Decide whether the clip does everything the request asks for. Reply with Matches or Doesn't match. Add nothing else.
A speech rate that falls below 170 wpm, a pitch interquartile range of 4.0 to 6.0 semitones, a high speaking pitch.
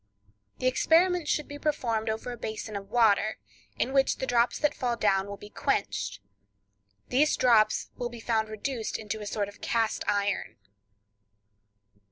Doesn't match